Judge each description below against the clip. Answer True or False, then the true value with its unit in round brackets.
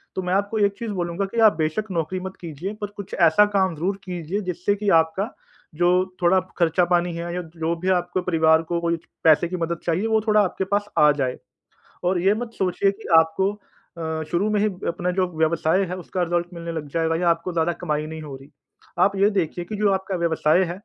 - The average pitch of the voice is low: False (175 Hz)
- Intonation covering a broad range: False (2.8 semitones)